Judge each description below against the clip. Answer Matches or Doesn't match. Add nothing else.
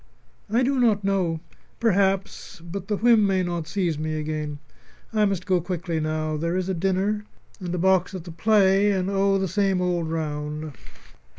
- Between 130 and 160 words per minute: Doesn't match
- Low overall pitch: Doesn't match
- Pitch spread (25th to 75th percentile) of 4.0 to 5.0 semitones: Doesn't match